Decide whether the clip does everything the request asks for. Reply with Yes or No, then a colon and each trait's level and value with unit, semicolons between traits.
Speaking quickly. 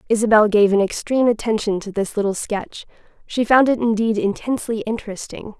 No: average, 160 wpm